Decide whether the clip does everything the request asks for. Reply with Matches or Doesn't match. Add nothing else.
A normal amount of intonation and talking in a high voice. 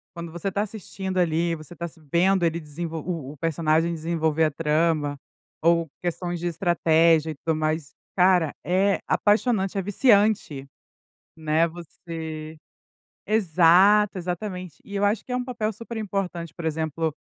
Doesn't match